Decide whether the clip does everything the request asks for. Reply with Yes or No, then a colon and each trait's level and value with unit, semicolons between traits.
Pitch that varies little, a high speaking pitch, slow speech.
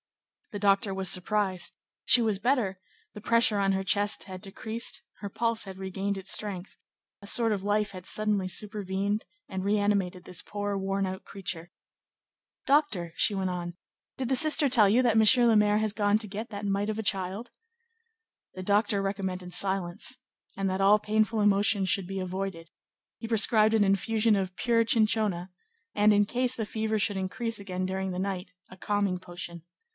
No: narrow, 2.3 semitones; high, 200 Hz; average, 180 wpm